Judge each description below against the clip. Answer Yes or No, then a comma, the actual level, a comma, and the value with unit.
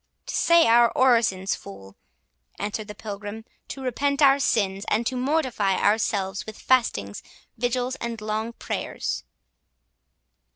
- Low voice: No, high, 225 Hz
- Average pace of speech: No, slow, 125 wpm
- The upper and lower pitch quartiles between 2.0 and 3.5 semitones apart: No, average, 4.0 semitones